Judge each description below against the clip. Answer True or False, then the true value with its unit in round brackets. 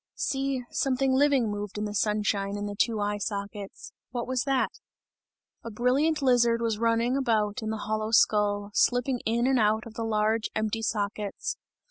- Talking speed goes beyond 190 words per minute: False (170 wpm)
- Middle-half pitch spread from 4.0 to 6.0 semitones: False (3.1 semitones)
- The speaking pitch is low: False (225 Hz)